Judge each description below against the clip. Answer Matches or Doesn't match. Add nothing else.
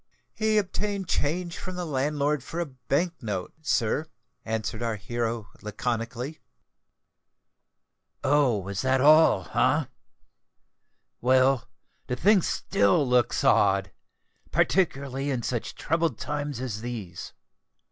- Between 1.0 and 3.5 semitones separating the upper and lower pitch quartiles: Doesn't match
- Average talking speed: Doesn't match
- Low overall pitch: Matches